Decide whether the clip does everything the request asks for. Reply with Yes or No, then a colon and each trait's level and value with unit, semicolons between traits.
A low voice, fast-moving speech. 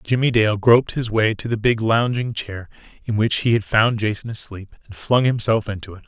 Yes: low, 110 Hz; fast, 215 wpm